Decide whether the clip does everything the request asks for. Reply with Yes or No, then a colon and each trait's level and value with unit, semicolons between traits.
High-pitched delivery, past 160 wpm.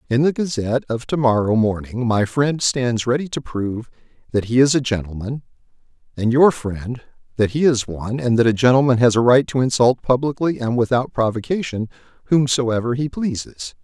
No: low, 125 Hz; average, 175 wpm